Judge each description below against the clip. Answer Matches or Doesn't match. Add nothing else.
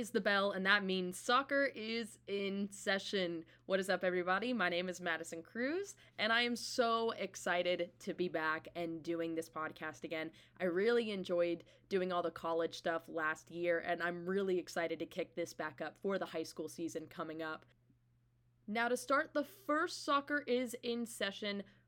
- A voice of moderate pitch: Matches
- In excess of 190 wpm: Doesn't match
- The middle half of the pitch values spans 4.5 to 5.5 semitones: Matches